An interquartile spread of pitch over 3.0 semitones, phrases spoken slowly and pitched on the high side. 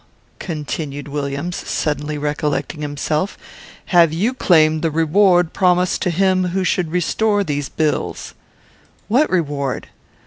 No: average, 3.7 semitones; slow, 115 wpm; medium, 160 Hz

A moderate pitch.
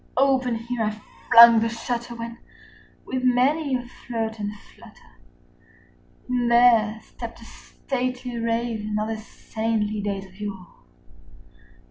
No: high, 230 Hz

